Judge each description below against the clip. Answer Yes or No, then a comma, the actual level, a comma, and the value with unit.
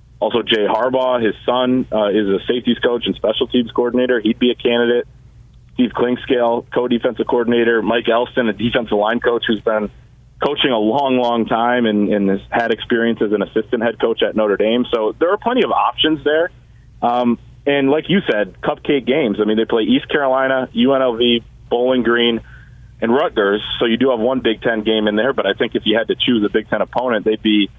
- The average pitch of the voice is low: Yes, low, 120 Hz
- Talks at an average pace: No, fast, 210 wpm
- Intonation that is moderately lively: No, narrow, 2.1 semitones